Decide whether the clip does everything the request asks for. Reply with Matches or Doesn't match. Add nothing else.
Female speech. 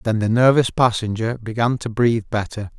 Doesn't match